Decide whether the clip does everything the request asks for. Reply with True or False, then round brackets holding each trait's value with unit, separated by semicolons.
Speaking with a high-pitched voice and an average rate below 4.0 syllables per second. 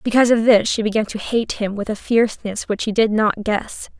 False (220 Hz; 5.5 syllables/s)